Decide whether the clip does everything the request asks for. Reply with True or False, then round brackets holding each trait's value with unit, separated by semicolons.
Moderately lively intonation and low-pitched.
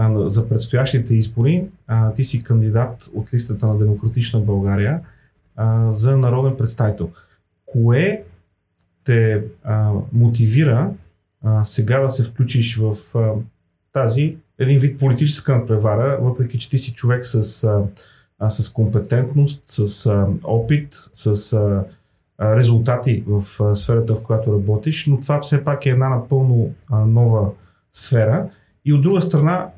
True (3.7 semitones; 115 Hz)